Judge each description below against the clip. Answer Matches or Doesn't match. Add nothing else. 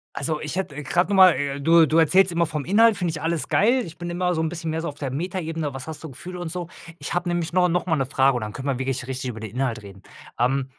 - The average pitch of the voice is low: Doesn't match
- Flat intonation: Doesn't match